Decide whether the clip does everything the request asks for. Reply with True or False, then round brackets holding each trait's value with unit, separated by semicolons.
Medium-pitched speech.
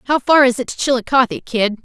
False (250 Hz)